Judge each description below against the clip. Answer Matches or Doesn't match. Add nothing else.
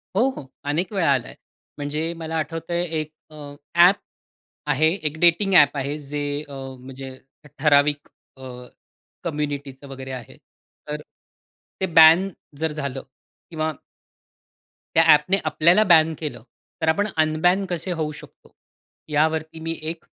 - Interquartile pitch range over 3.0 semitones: Doesn't match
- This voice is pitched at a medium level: Matches